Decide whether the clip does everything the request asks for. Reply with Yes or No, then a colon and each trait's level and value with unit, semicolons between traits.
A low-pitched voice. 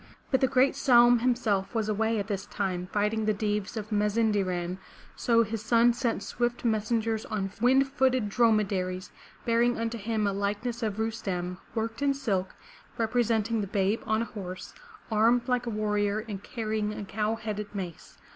No: high, 220 Hz